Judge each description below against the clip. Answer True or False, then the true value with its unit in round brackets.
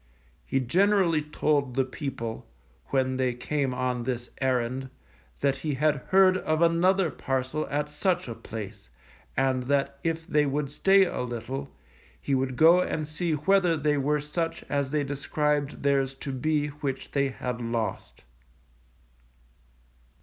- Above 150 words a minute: False (145 wpm)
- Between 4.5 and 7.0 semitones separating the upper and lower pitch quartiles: False (2.9 semitones)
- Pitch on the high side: False (140 Hz)